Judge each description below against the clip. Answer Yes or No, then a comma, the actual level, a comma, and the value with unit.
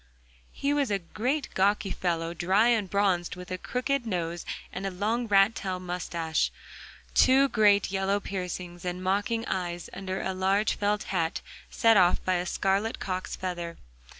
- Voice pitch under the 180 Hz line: No, high, 190 Hz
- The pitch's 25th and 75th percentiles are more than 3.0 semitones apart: No, average, 2.7 semitones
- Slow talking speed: No, average, 155 wpm